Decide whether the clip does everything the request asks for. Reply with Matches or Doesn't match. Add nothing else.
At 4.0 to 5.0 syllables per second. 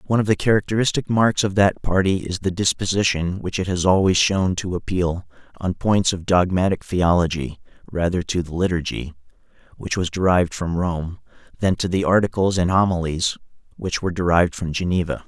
Doesn't match